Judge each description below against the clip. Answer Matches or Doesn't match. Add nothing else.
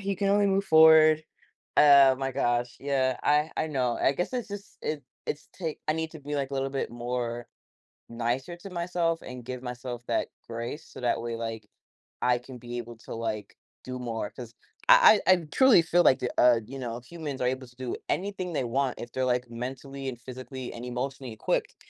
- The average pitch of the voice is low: Matches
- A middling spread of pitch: Matches